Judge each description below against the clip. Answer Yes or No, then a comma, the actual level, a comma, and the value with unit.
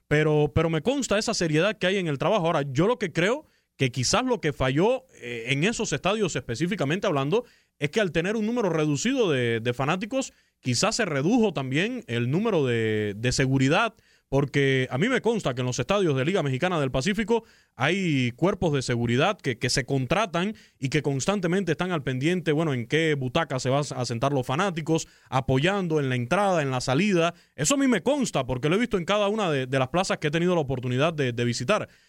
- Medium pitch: Yes, medium, 155 Hz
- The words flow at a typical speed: No, fast, 215 wpm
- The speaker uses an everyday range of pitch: No, wide, 6.8 semitones